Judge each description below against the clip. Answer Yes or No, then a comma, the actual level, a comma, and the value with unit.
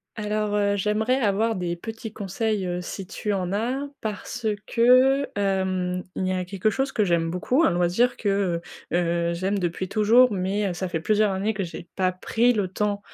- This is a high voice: Yes, high, 200 Hz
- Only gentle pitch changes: No, average, 3.3 semitones